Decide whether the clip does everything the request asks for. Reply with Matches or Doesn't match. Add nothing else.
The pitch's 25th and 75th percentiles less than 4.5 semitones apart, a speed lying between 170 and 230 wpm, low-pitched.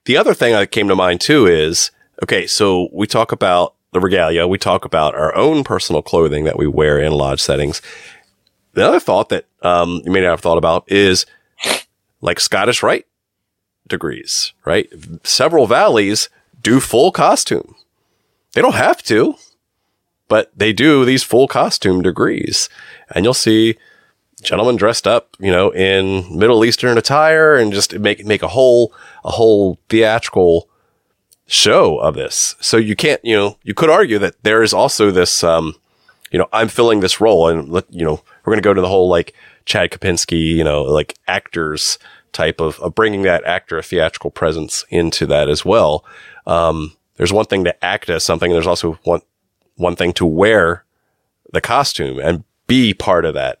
Doesn't match